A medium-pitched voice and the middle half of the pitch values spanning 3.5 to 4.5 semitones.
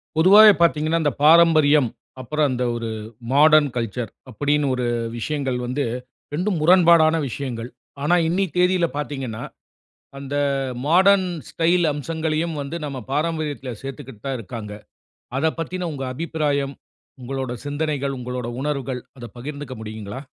Yes: medium, 145 Hz; average, 3.9 semitones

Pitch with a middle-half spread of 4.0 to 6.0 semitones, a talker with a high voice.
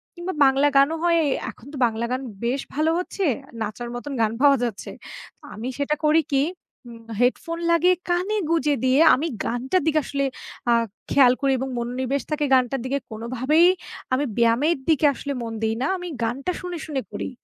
Yes: average, 4.5 semitones; very high, 275 Hz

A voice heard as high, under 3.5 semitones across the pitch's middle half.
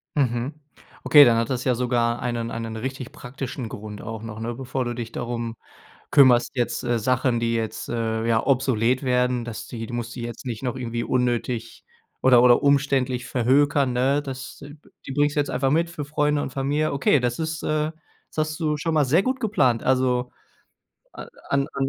No: low, 125 Hz; average, 3.0 semitones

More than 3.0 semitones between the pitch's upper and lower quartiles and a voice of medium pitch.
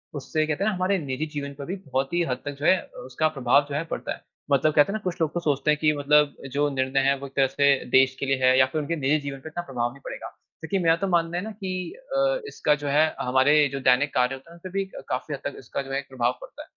Yes: average, 3.6 semitones; medium, 145 Hz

